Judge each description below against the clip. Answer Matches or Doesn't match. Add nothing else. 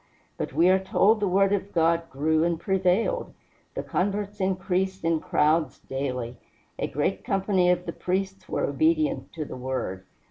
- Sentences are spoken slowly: Doesn't match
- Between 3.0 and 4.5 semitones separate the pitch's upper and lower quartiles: Matches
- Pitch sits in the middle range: Matches